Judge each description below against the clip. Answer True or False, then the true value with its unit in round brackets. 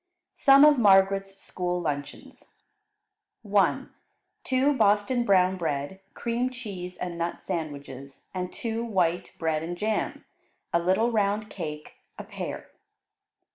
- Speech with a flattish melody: False (4.5 semitones)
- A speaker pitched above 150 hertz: True (190 Hz)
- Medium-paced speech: False (120 wpm)